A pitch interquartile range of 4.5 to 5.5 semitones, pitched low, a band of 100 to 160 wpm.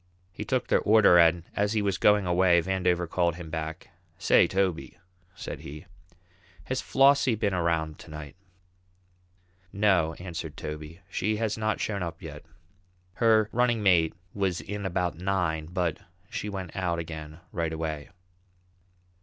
No: average, 3.7 semitones; very low, 90 Hz; average, 145 wpm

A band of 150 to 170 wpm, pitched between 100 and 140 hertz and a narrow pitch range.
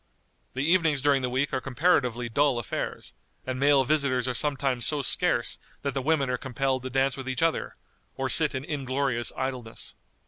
No: average, 180 wpm; low, 135 Hz; narrow, 2.1 semitones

